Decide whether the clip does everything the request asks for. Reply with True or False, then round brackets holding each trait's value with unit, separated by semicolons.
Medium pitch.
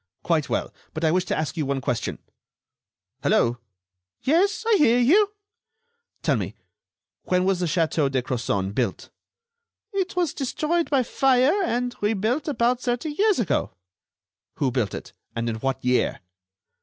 False (215 Hz)